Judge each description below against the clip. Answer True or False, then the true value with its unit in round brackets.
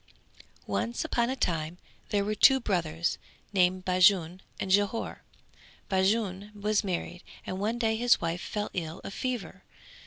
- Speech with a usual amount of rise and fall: True (3.2 semitones)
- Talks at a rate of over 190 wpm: False (145 wpm)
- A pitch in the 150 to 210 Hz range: True (190 Hz)